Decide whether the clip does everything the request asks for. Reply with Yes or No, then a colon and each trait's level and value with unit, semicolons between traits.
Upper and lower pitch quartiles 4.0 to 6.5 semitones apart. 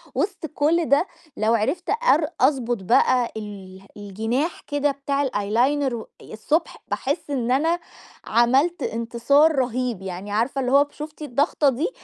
Yes: average, 4.4 semitones